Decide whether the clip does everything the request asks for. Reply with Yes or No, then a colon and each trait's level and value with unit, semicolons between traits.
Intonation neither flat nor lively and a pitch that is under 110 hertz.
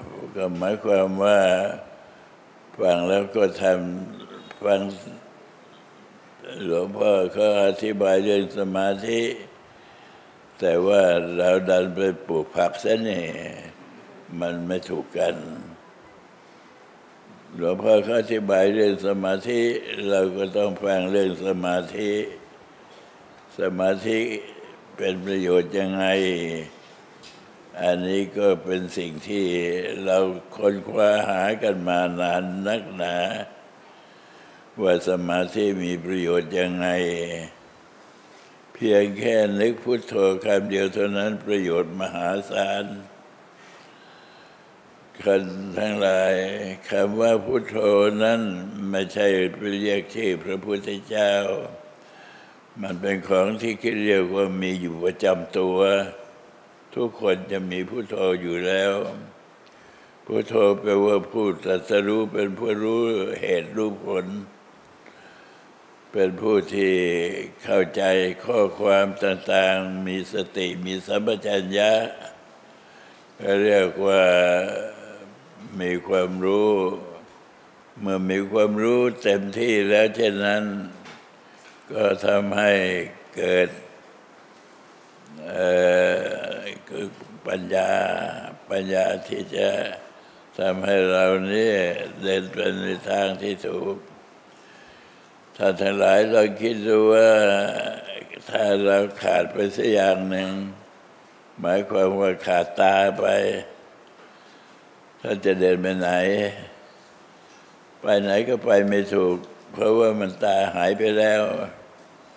No: narrow, 1.7 semitones; very low, 95 Hz